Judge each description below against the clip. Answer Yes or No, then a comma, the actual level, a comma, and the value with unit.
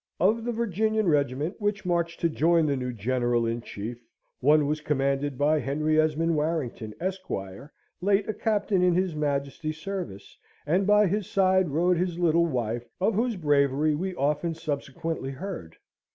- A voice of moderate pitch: Yes, medium, 155 Hz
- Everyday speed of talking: Yes, average, 160 wpm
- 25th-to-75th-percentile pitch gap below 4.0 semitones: No, average, 5.1 semitones